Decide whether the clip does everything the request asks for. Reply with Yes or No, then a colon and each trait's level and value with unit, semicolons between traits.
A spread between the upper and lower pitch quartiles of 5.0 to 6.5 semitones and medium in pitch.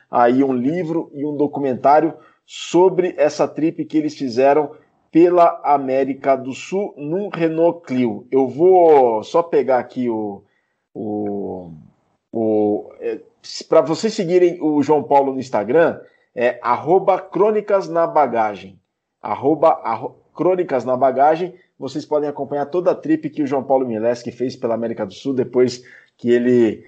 Yes: wide, 5.6 semitones; medium, 145 Hz